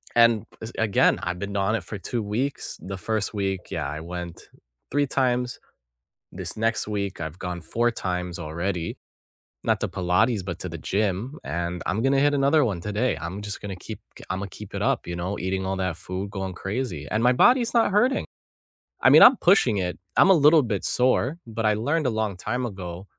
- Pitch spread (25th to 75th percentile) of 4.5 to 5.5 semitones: Yes, average, 5.1 semitones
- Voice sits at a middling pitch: No, low, 100 Hz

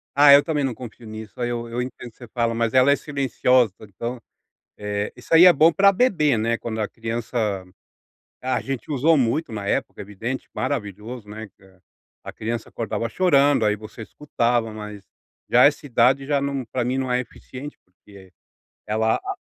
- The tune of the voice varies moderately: Yes, average, 4.0 semitones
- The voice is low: Yes, low, 120 Hz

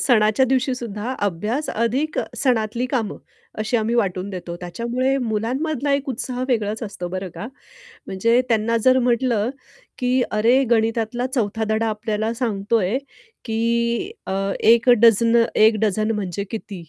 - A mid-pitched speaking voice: No, high, 230 Hz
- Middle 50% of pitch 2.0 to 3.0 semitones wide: Yes, average, 2.7 semitones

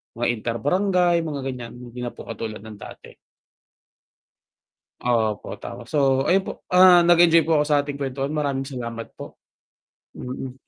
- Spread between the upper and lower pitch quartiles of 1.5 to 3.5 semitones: No, wide, 5.4 semitones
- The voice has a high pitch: No, low, 135 Hz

